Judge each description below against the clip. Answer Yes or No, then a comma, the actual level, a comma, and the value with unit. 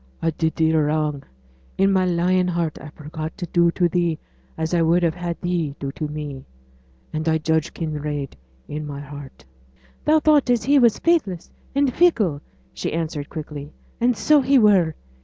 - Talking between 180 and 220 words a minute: Yes, average, 185 wpm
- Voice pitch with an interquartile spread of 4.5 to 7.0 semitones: No, average, 3.6 semitones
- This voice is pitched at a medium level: Yes, medium, 165 Hz